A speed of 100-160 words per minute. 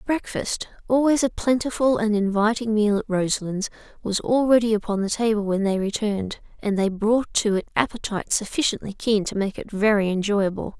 Yes: average, 155 wpm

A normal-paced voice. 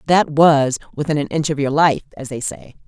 No: fast, 230 wpm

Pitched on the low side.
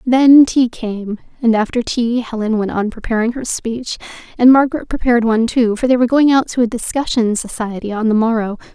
No: high, 235 Hz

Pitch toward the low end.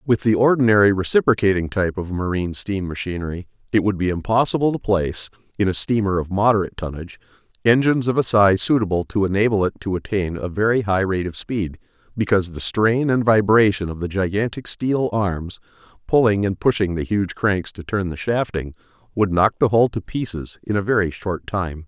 Yes: low, 100 Hz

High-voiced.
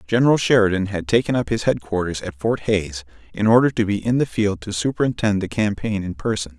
No: low, 105 Hz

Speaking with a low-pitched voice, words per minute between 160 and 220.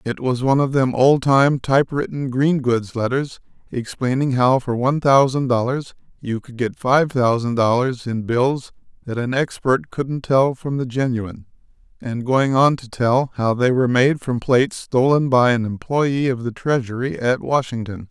Yes: low, 130 Hz; average, 175 wpm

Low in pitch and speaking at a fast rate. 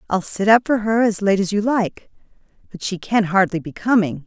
No: high, 200 Hz; fast, 225 wpm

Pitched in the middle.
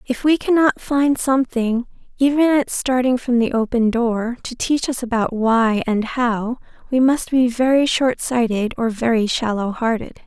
No: high, 245 Hz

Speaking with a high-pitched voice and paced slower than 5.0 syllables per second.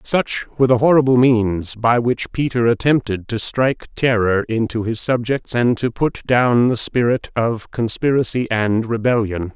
No: low, 120 Hz; 4.4 syllables/s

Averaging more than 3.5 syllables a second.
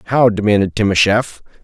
Yes: 5.8 syllables/s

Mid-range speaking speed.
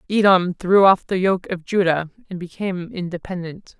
Yes: average, 160 wpm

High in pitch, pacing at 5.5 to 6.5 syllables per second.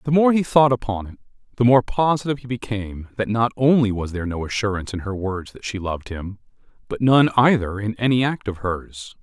No: low, 110 Hz; 5.9 syllables/s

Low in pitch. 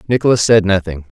Yes: low, 100 Hz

